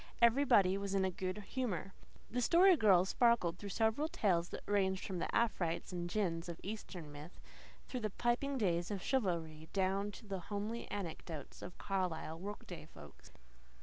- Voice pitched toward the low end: No, high, 195 Hz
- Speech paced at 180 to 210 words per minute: No, average, 160 wpm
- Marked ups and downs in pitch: No, average, 4.2 semitones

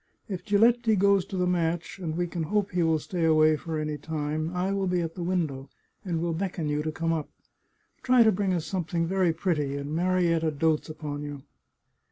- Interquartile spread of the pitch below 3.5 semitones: Yes, average, 3.0 semitones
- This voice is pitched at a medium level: Yes, medium, 165 Hz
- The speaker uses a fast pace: Yes, fast, 210 wpm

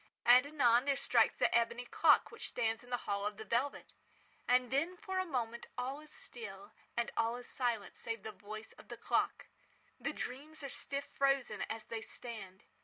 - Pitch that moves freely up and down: No, average, 3.5 semitones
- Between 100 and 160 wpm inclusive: No, average, 190 wpm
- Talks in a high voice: Yes, high, 245 Hz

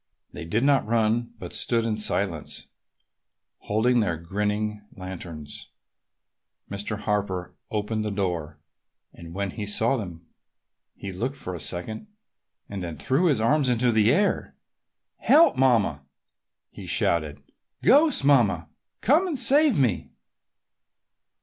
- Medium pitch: No, low, 105 Hz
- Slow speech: Yes, slow, 130 wpm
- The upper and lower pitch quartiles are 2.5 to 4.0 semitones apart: No, wide, 5.4 semitones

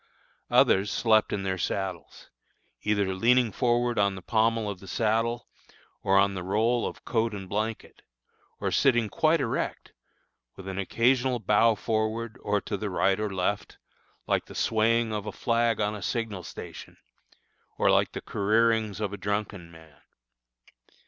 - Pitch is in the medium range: No, low, 105 Hz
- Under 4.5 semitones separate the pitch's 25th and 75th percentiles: Yes, average, 2.8 semitones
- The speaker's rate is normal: Yes, average, 155 wpm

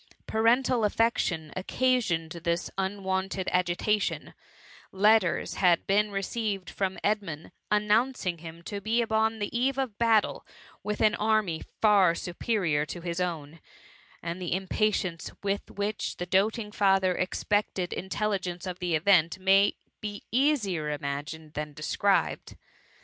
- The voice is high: Yes, high, 195 Hz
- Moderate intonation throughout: Yes, average, 3.6 semitones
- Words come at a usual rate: No, slow, 130 wpm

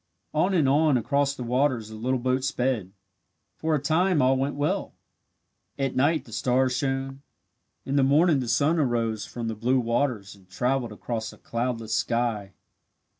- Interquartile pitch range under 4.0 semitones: Yes, average, 3.3 semitones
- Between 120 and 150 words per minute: No, average, 170 wpm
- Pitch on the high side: No, low, 130 Hz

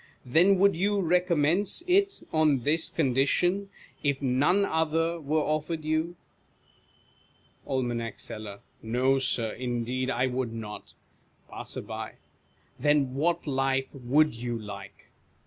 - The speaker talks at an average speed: No, slow, 115 wpm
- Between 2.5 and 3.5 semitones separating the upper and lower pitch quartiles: No, average, 4.9 semitones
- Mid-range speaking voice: Yes, medium, 145 Hz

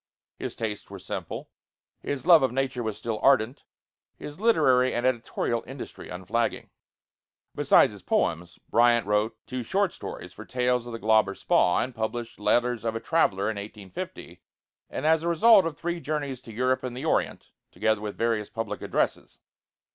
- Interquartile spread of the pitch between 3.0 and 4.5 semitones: Yes, average, 3.7 semitones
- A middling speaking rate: Yes, average, 165 wpm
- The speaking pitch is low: Yes, low, 120 Hz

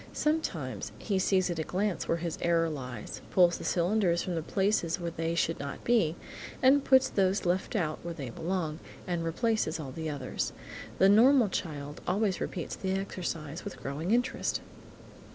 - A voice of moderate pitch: Yes, medium, 175 Hz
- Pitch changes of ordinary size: Yes, average, 3.8 semitones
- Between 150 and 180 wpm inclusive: Yes, average, 170 wpm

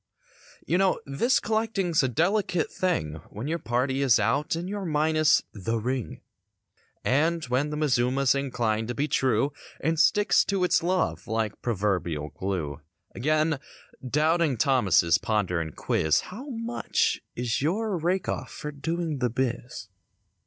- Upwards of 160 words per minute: No, average, 145 wpm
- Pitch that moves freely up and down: Yes, wide, 6.9 semitones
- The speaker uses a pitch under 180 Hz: Yes, medium, 140 Hz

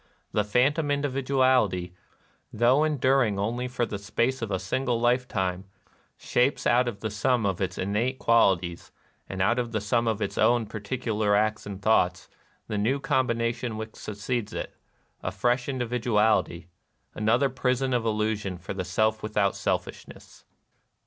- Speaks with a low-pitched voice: Yes, low, 115 Hz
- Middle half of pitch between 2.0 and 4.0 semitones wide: Yes, average, 3.6 semitones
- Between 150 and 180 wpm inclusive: Yes, average, 160 wpm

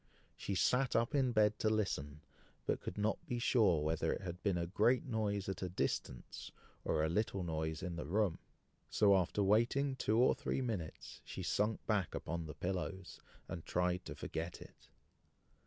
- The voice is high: No, very low, 95 Hz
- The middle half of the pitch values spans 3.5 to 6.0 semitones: Yes, average, 4.5 semitones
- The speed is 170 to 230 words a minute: Yes, average, 180 wpm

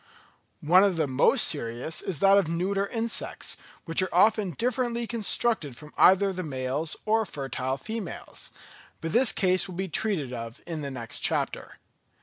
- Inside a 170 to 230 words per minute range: No, average, 160 wpm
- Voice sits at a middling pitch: Yes, medium, 180 Hz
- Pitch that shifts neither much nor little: No, wide, 6.3 semitones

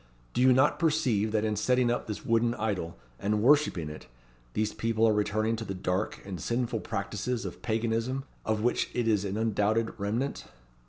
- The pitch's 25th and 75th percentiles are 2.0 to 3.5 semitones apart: Yes, narrow, 2.5 semitones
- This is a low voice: Yes, low, 110 Hz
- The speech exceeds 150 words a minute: Yes, average, 180 wpm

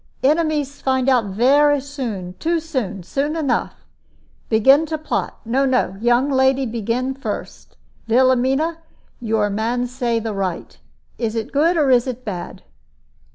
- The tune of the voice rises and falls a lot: No, average, 3.7 semitones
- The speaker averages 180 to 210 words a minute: No, average, 140 wpm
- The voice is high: Yes, very high, 255 Hz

